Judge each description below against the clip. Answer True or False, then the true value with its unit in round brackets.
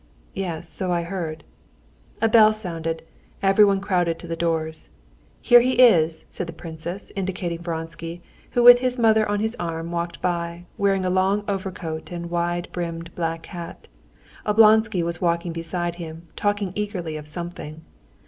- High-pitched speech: False (175 Hz)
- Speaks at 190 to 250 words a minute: False (155 wpm)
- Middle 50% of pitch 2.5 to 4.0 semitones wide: True (3.1 semitones)